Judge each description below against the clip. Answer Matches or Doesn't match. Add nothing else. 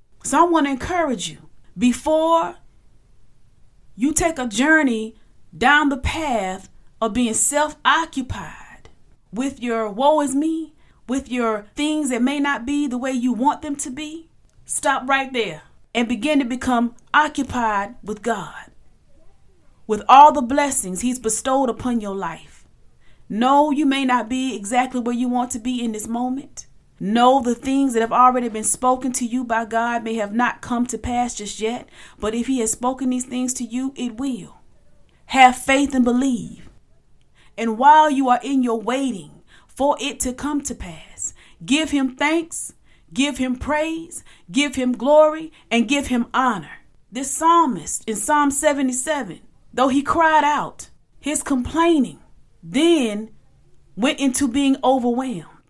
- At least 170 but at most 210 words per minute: Doesn't match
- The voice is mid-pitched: Doesn't match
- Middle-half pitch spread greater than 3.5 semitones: Doesn't match